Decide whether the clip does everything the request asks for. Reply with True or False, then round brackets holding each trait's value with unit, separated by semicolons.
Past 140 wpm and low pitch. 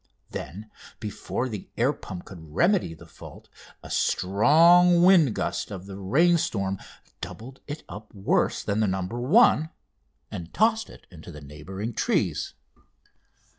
False (135 wpm; 105 Hz)